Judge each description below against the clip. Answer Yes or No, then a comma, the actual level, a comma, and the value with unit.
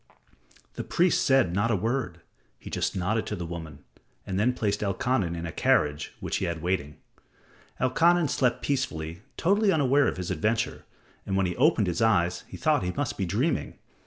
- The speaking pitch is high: No, low, 100 Hz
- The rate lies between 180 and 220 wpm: Yes, average, 190 wpm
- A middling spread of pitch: No, wide, 6.9 semitones